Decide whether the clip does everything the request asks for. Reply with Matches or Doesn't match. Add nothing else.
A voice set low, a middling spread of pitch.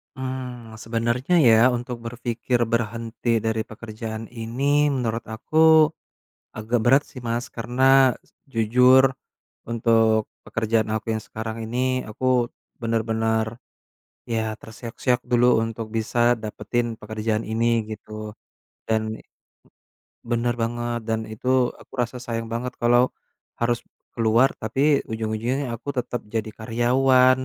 Doesn't match